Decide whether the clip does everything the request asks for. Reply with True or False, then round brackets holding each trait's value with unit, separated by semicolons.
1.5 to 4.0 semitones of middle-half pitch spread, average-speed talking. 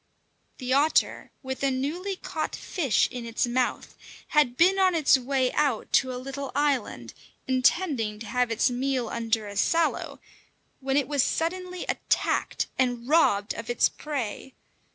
True (3.7 semitones; 155 wpm)